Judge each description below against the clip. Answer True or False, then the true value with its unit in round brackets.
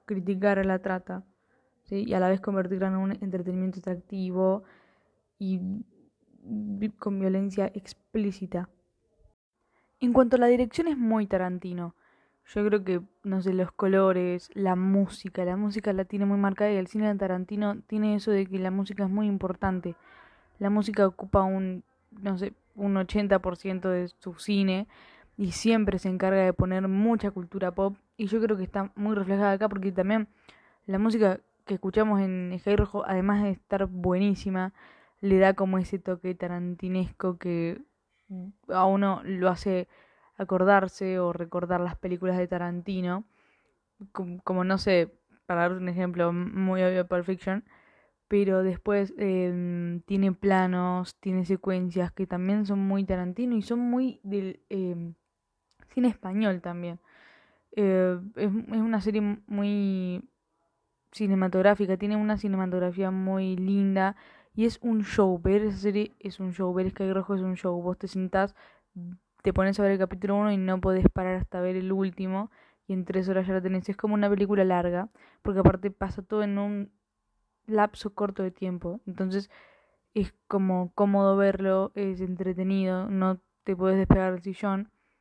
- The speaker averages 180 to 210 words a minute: False (160 wpm)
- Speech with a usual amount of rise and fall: False (1.7 semitones)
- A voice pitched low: False (195 Hz)